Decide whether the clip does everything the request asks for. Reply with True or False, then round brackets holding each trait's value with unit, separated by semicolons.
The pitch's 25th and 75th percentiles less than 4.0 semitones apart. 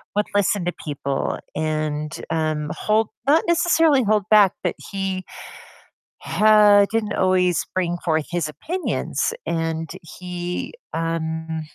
False (4.6 semitones)